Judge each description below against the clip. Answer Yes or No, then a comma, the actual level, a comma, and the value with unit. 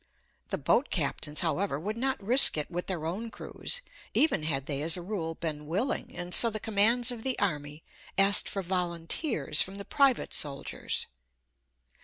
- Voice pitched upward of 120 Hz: Yes, medium, 185 Hz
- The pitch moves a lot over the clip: Yes, wide, 6.0 semitones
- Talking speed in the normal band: Yes, average, 170 wpm